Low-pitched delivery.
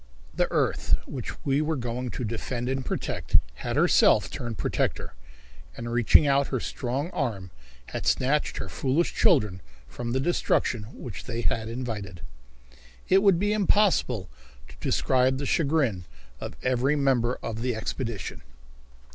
Yes: low, 125 Hz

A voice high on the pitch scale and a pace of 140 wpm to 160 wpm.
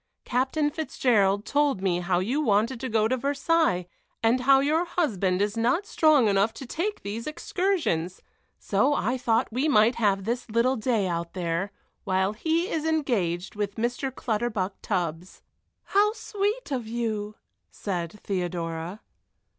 Yes: high, 230 Hz; average, 145 wpm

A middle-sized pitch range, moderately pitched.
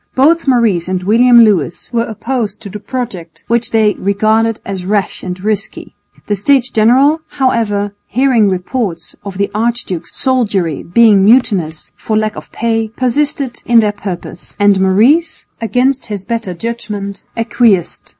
No: average, 3.5 semitones; high, 215 Hz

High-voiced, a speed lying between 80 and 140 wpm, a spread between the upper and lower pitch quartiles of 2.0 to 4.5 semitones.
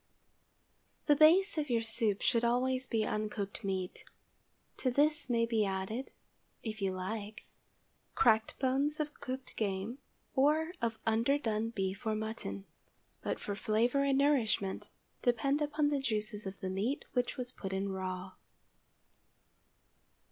No: high, 230 Hz; slow, 135 wpm; average, 5.0 semitones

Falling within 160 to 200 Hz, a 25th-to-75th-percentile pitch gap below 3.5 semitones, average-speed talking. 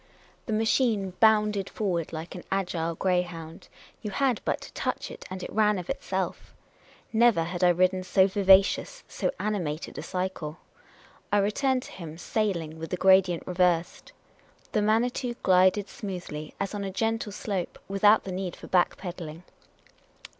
Yes: high, 190 Hz; average, 3.1 semitones; average, 160 wpm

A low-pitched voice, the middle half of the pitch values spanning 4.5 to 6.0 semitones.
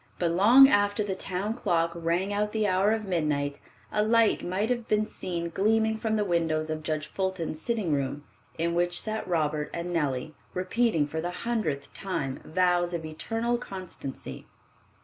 No: medium, 180 Hz; average, 5.0 semitones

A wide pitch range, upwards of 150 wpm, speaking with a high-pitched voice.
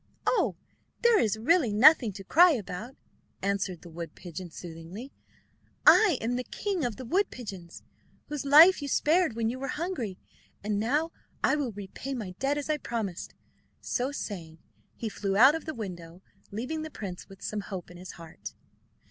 Yes: wide, 7.4 semitones; average, 175 wpm; high, 230 Hz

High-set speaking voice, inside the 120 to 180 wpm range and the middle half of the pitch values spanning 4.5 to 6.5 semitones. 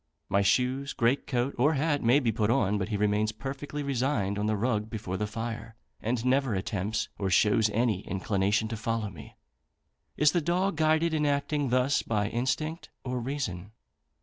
No: low, 115 Hz; average, 175 wpm; average, 5.0 semitones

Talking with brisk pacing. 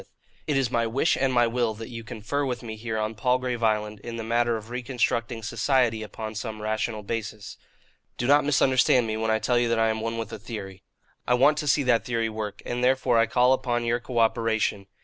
Yes: fast, 220 wpm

